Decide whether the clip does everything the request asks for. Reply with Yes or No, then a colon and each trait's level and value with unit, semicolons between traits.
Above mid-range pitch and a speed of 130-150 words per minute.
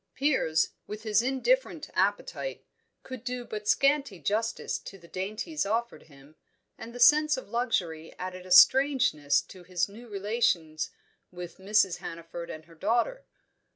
Yes: high, 210 Hz; average, 145 wpm